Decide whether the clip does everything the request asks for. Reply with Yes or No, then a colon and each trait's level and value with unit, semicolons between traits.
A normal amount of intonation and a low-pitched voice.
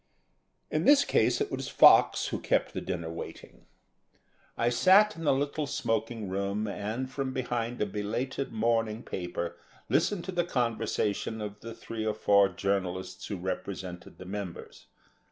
Yes: average, 4.0 semitones; low, 110 Hz